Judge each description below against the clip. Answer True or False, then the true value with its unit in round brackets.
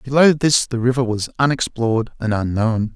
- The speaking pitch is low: True (120 Hz)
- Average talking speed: True (160 wpm)